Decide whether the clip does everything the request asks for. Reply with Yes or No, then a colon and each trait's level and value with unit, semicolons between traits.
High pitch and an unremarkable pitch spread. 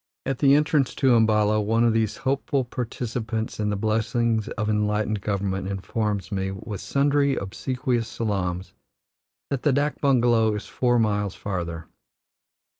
No: low, 110 Hz; average, 3.3 semitones